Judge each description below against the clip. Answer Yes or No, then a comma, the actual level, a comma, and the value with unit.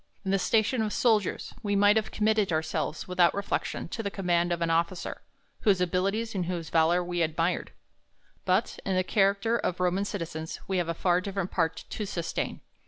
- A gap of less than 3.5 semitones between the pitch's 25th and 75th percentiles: Yes, average, 2.9 semitones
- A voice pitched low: No, medium, 185 Hz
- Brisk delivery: No, average, 185 wpm